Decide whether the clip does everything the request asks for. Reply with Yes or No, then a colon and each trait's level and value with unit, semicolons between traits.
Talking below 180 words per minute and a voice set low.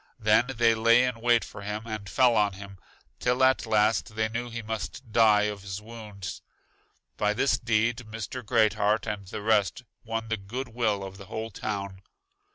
No: average, 185 wpm; low, 110 Hz